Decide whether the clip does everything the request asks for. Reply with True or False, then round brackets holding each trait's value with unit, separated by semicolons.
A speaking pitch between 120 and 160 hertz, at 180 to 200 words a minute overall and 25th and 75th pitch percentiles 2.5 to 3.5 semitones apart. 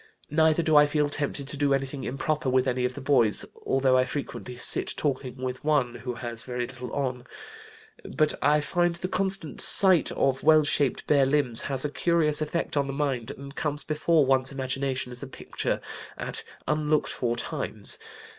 True (140 Hz; 185 wpm; 2.8 semitones)